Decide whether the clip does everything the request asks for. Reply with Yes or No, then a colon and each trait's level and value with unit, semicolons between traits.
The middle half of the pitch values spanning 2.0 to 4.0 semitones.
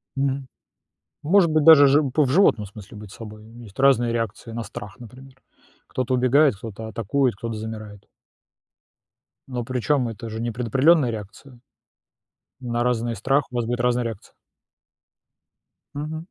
Yes: average, 3.5 semitones